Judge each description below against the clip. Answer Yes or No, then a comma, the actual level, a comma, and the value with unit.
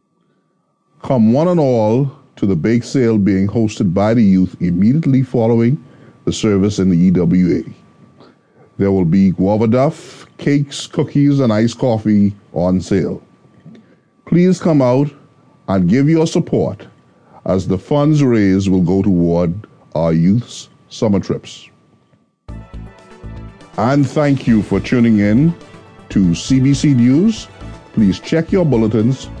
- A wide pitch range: Yes, wide, 6.5 semitones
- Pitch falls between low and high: No, low, 115 Hz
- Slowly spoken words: Yes, slow, 130 wpm